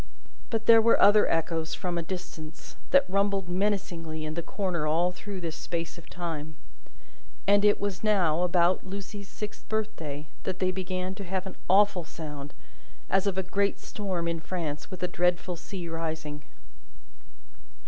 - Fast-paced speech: No, average, 165 wpm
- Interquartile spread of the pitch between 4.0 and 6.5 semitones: No, average, 3.3 semitones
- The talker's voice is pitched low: No, medium, 180 Hz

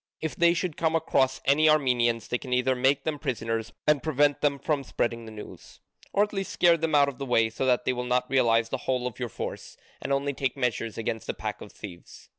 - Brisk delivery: Yes, fast, 235 wpm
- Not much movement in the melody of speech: No, average, 3.3 semitones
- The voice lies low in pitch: Yes, low, 130 Hz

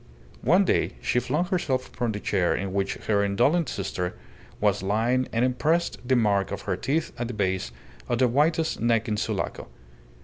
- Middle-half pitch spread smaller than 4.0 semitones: No, average, 4.5 semitones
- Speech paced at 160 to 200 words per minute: Yes, average, 180 wpm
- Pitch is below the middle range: Yes, low, 115 Hz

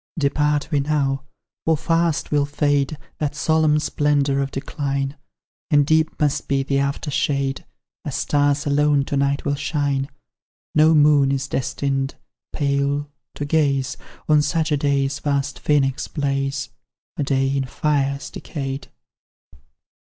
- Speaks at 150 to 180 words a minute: No, slow, 135 wpm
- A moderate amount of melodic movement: No, narrow, 1.2 semitones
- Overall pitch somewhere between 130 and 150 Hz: Yes, medium, 140 Hz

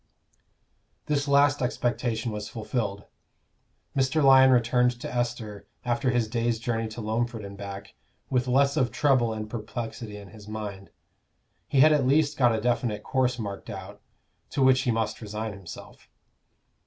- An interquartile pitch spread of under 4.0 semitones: Yes, average, 3.2 semitones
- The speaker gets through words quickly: No, average, 155 wpm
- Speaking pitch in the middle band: No, low, 120 Hz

